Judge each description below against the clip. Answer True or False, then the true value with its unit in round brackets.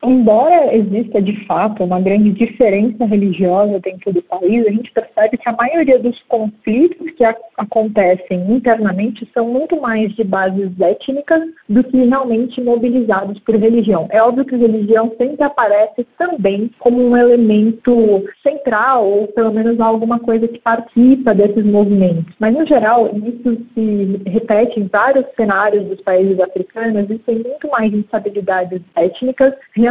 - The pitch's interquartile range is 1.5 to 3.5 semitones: True (3.0 semitones)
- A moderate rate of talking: True (150 wpm)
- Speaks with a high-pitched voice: True (225 Hz)